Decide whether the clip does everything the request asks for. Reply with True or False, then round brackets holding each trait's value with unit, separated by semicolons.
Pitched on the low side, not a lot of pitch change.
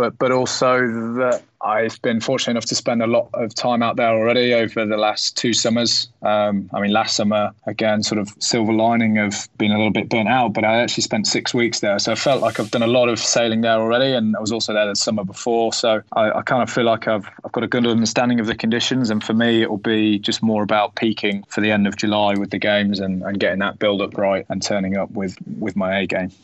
True (110 Hz; 2.1 semitones)